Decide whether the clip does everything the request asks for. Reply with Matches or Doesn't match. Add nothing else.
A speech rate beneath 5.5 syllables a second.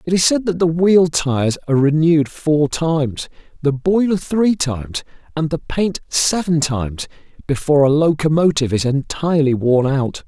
Matches